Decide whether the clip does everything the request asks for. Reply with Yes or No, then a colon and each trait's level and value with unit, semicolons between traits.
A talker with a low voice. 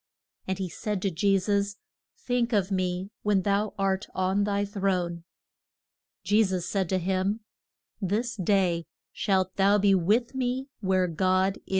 No: high, 195 Hz